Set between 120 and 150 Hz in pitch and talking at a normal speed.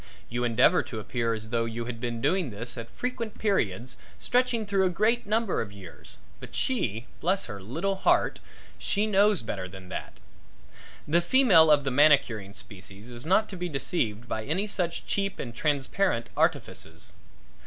Yes: medium, 140 Hz; average, 170 wpm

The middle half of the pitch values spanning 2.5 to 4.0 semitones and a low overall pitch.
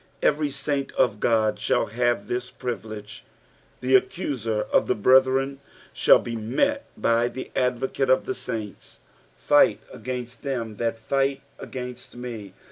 Yes: average, 2.8 semitones; low, 125 Hz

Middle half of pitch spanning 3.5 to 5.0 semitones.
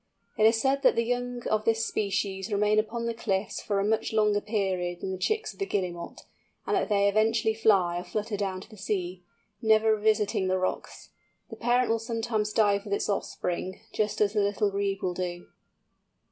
No: narrow, 2.4 semitones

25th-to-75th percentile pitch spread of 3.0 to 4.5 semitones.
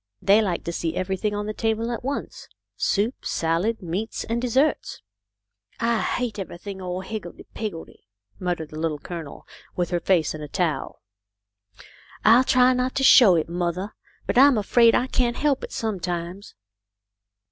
No: average, 5.1 semitones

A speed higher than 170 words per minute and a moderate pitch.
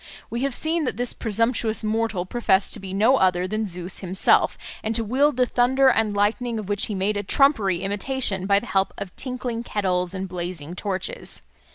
No: average, 195 wpm; high, 210 Hz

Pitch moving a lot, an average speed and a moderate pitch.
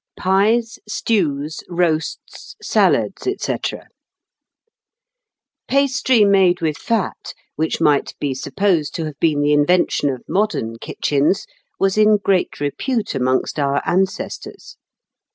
No: wide, 5.9 semitones; slow, 110 wpm; medium, 175 Hz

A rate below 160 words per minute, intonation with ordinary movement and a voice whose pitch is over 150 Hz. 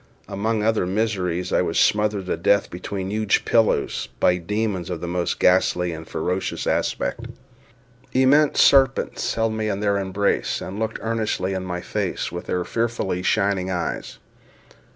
No: average, 150 wpm; average, 3.4 semitones; low, 100 Hz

